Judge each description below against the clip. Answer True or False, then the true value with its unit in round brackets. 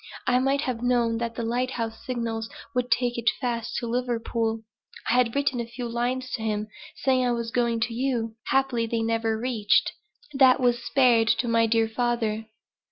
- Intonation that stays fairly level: True (1.6 semitones)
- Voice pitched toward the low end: False (235 Hz)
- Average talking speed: True (180 wpm)